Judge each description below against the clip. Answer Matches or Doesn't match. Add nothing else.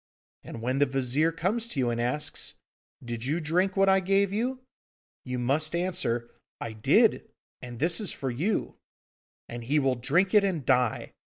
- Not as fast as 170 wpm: Doesn't match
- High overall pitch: Doesn't match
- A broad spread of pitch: Matches